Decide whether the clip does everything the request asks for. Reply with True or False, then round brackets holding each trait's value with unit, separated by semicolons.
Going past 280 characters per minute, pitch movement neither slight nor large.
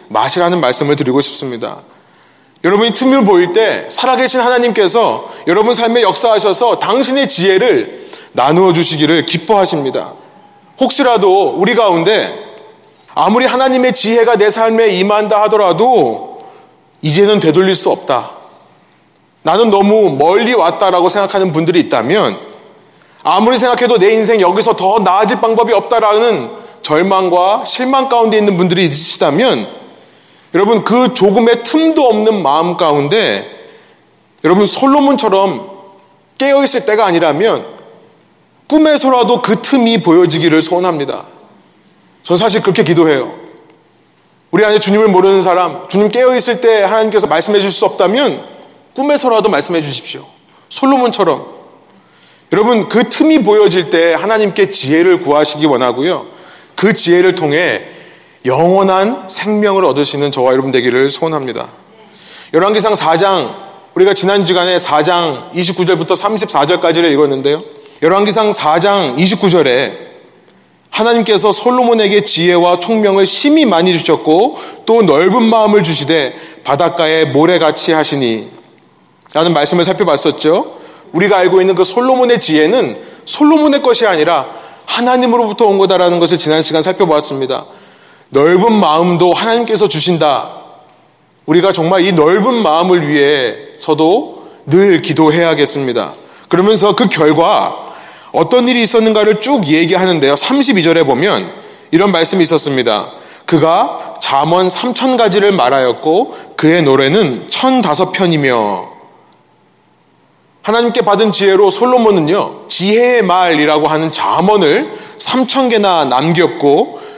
False (300 characters per minute; 5.7 semitones)